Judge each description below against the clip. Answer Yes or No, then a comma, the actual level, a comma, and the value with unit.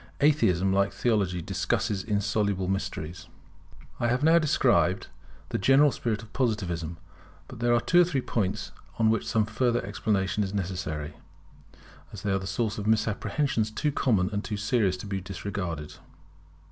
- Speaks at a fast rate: No, average, 160 wpm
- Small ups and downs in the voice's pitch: No, average, 3.8 semitones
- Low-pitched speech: Yes, low, 105 Hz